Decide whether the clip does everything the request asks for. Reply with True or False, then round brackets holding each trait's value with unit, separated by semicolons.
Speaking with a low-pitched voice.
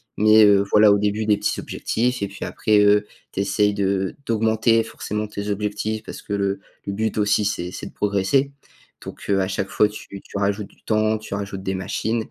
True (105 Hz)